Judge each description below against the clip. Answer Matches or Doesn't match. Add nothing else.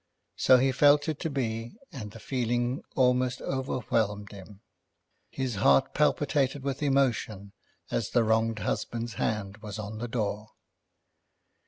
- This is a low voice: Matches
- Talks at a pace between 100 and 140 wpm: Matches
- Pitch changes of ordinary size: Matches